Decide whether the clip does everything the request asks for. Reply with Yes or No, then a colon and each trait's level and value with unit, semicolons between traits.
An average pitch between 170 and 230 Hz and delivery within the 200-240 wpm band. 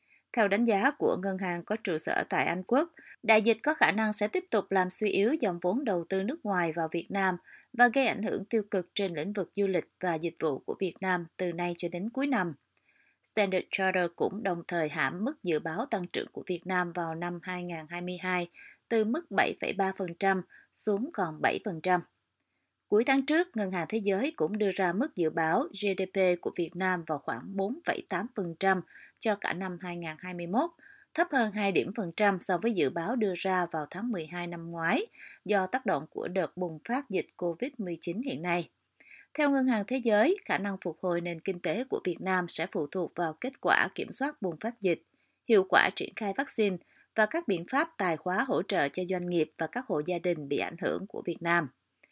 Yes: high, 190 Hz; average, 210 wpm